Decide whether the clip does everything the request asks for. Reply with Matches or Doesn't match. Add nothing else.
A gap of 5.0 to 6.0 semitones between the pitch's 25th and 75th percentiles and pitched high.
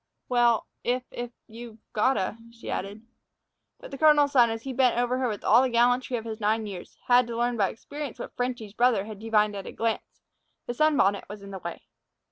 Doesn't match